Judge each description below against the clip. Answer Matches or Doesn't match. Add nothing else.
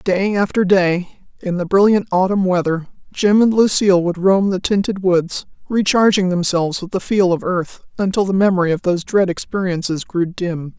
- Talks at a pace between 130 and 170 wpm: Doesn't match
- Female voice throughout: Matches